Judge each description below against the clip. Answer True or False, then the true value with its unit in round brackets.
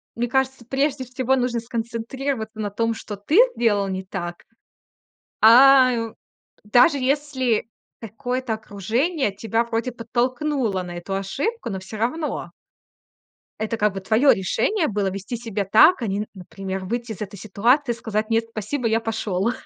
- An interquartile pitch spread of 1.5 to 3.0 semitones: False (3.8 semitones)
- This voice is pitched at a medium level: False (230 Hz)